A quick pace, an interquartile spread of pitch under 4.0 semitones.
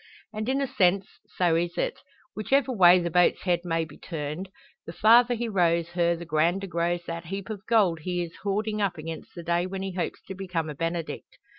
Yes: fast, 210 wpm; average, 2.8 semitones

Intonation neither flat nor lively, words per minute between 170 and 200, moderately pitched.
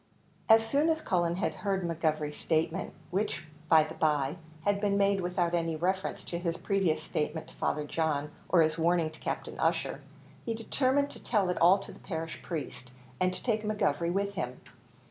Yes: average, 3.9 semitones; average, 185 wpm; medium, 175 Hz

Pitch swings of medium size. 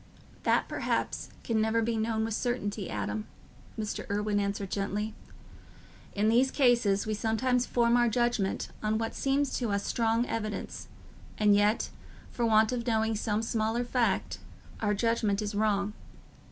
No: narrow, 2.2 semitones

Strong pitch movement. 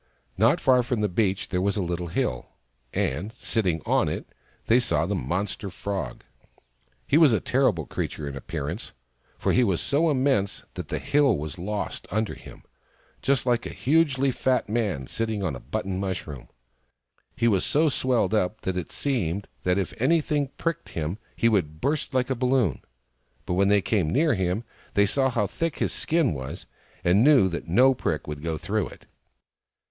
Yes: wide, 6.5 semitones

